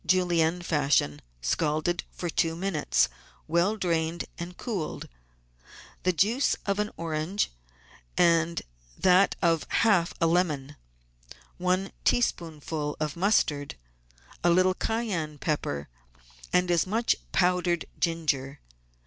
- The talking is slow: Yes, slow, 105 wpm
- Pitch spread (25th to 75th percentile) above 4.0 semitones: No, average, 2.9 semitones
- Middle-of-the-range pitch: Yes, medium, 170 Hz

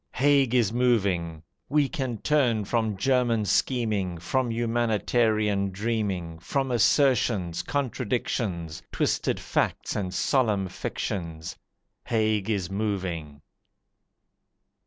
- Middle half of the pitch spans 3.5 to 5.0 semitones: Yes, average, 4.7 semitones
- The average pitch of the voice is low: Yes, low, 110 Hz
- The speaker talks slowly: Yes, slow, 95 wpm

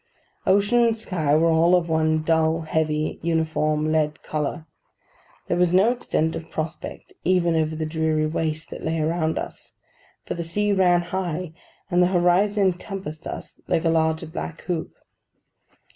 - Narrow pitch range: Yes, narrow, 2.2 semitones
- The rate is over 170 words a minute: No, average, 160 wpm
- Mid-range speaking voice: Yes, medium, 165 Hz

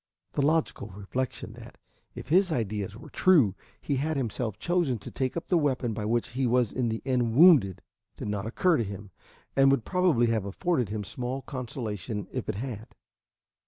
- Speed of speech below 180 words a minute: No, average, 185 wpm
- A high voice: No, low, 125 Hz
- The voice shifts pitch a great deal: No, average, 4.7 semitones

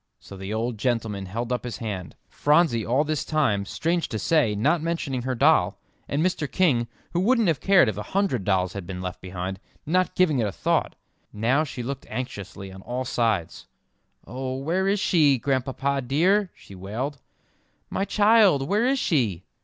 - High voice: No, low, 130 Hz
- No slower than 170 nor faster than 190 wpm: Yes, average, 180 wpm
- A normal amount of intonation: No, wide, 7.4 semitones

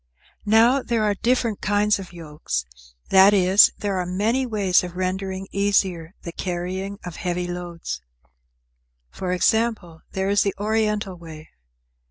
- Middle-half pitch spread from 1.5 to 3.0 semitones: Yes, average, 2.7 semitones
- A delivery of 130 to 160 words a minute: Yes, average, 140 wpm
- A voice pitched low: No, high, 190 Hz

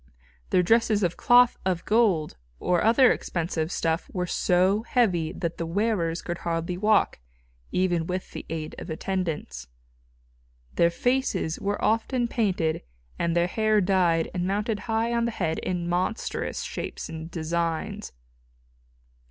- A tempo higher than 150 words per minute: No, average, 140 wpm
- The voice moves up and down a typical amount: Yes, average, 4.5 semitones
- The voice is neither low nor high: Yes, medium, 180 Hz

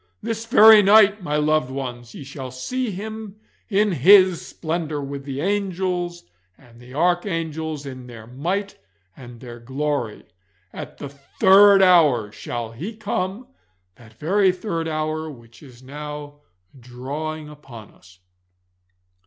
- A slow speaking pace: Yes, slow, 130 wpm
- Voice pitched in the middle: Yes, medium, 155 Hz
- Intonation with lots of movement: Yes, wide, 6.6 semitones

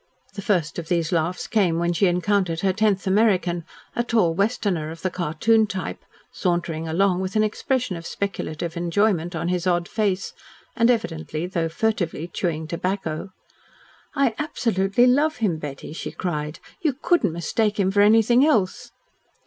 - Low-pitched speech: No, medium, 185 Hz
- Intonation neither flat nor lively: Yes, average, 4.3 semitones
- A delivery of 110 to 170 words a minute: Yes, average, 155 wpm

